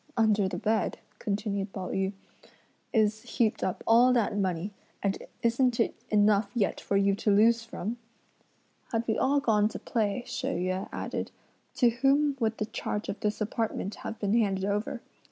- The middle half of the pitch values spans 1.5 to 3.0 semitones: Yes, narrow, 2.5 semitones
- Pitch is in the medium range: No, high, 215 Hz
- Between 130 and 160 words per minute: No, average, 170 wpm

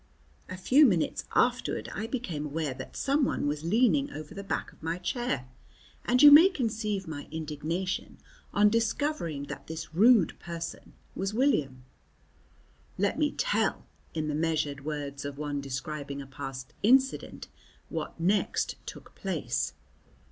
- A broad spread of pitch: Yes, wide, 7.4 semitones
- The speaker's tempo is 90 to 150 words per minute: Yes, average, 140 wpm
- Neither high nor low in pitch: Yes, medium, 165 Hz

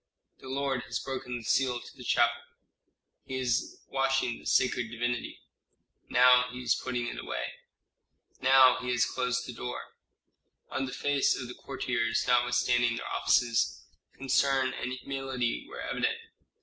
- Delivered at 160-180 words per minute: No, average, 150 wpm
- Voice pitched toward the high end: No, low, 125 Hz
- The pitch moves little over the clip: Yes, narrow, 1.6 semitones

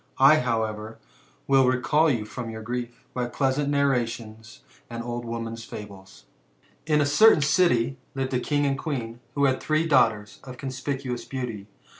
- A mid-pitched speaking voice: No, low, 125 Hz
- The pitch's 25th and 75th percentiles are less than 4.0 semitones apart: Yes, average, 3.6 semitones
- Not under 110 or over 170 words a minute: Yes, average, 160 wpm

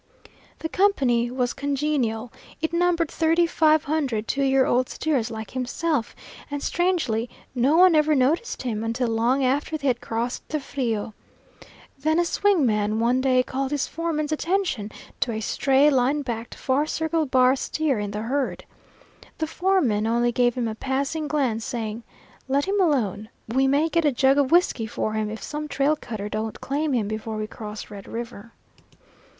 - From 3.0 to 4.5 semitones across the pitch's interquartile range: No, average, 5.1 semitones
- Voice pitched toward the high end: Yes, very high, 265 Hz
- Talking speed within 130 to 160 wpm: No, average, 175 wpm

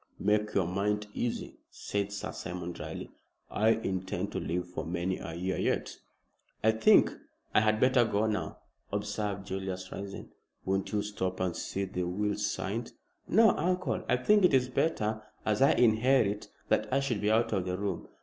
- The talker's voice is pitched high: No, low, 105 Hz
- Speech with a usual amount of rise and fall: Yes, average, 3.0 semitones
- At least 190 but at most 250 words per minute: No, average, 175 wpm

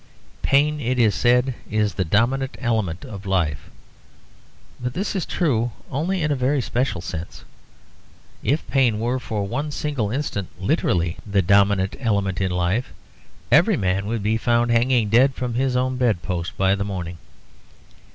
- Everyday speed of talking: Yes, average, 160 wpm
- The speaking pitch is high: No, low, 115 Hz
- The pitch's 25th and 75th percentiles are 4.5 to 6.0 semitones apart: Yes, average, 4.9 semitones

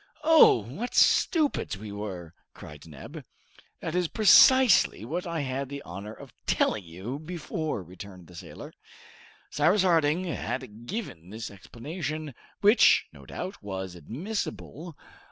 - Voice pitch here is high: No, low, 135 Hz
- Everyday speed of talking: No, slow, 130 wpm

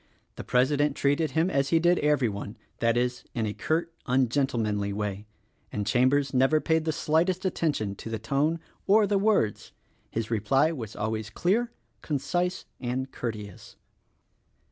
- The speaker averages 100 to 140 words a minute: No, average, 155 wpm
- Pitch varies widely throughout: Yes, wide, 6.2 semitones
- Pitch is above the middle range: No, low, 135 Hz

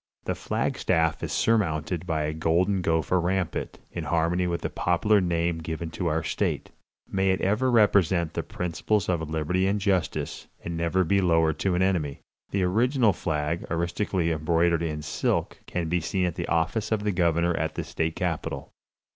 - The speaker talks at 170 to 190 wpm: Yes, average, 180 wpm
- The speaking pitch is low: Yes, very low, 85 Hz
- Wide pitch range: No, narrow, 2.6 semitones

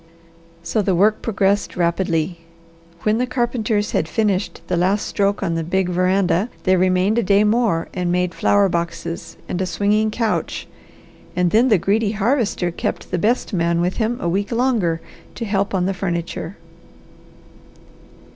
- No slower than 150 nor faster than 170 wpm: Yes, average, 160 wpm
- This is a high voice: Yes, high, 195 Hz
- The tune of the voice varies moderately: Yes, average, 3.4 semitones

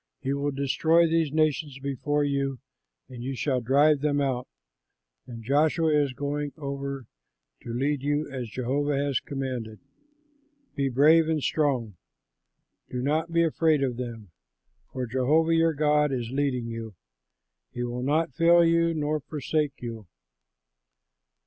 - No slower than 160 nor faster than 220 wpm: No, average, 140 wpm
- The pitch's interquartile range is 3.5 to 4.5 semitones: No, average, 3.1 semitones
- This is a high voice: No, medium, 140 Hz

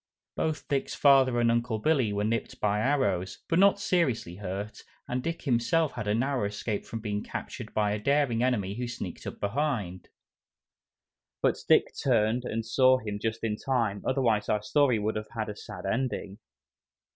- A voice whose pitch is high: No, low, 115 Hz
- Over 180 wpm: No, average, 175 wpm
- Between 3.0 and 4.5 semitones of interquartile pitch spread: Yes, average, 3.9 semitones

